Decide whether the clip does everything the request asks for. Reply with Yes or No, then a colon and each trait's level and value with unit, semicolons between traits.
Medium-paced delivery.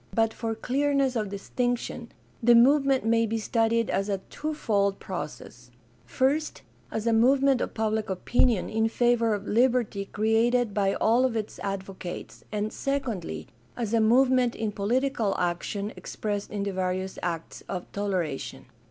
Yes: average, 145 wpm